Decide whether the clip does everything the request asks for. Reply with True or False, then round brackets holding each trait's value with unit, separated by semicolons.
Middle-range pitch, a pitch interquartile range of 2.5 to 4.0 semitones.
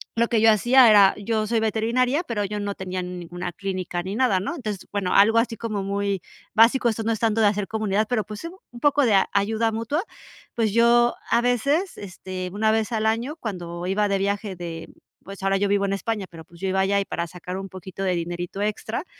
False (205 Hz; 3.0 semitones)